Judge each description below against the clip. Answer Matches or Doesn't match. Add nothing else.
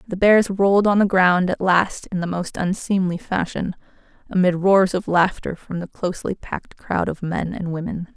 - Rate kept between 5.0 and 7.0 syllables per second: Doesn't match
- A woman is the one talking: Matches